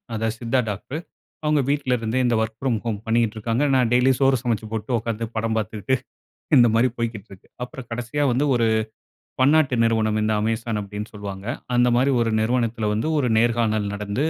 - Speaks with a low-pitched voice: Yes, low, 115 Hz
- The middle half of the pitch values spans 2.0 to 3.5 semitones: Yes, narrow, 2.4 semitones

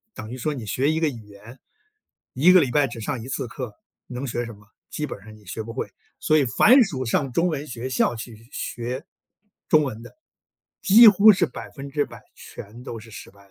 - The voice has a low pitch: Yes, low, 130 Hz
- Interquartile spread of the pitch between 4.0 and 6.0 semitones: Yes, average, 4.8 semitones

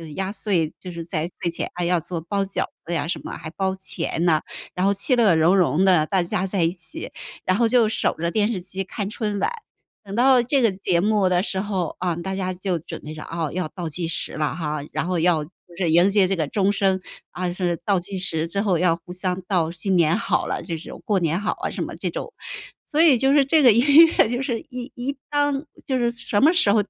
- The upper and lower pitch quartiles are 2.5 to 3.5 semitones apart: No, average, 3.9 semitones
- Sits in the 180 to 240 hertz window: Yes, high, 190 Hz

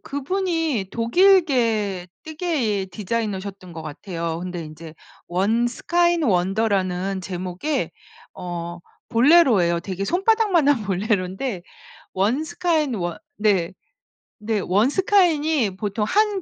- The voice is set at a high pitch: Yes, high, 215 Hz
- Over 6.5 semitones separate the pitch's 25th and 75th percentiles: Yes, wide, 8.9 semitones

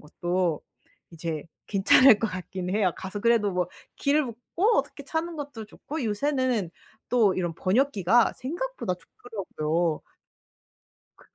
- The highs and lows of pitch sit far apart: Yes, wide, 6.4 semitones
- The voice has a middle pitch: No, high, 210 Hz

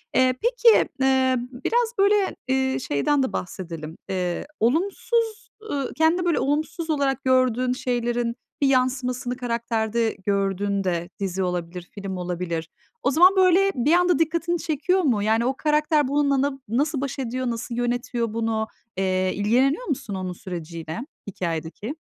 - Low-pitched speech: No, very high, 250 Hz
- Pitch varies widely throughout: Yes, wide, 6.8 semitones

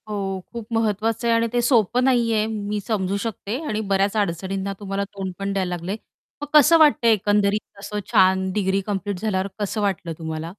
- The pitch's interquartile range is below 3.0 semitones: Yes, narrow, 2.6 semitones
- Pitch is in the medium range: No, high, 205 Hz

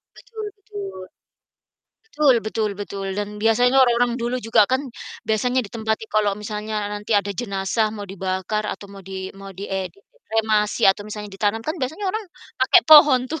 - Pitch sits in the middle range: No, high, 220 Hz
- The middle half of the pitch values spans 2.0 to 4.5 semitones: Yes, average, 3.7 semitones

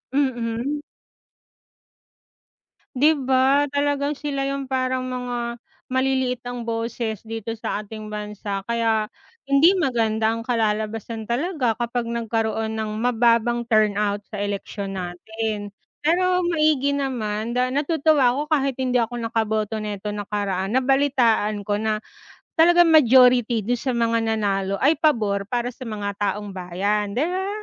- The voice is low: No, high, 235 Hz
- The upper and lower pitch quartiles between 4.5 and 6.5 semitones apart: No, average, 3.9 semitones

